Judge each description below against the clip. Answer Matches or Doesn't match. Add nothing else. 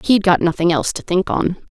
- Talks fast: Matches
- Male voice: Doesn't match